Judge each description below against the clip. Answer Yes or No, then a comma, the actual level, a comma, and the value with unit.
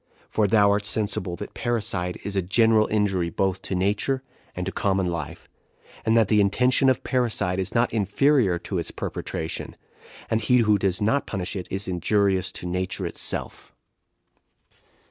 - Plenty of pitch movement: No, average, 3.2 semitones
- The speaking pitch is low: Yes, low, 100 Hz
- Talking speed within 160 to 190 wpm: Yes, average, 165 wpm